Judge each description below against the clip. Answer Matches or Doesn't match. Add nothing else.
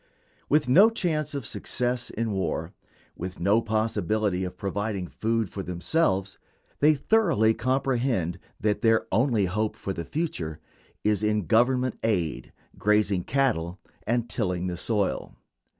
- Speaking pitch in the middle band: Doesn't match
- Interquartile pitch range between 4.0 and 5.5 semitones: Matches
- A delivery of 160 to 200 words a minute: Doesn't match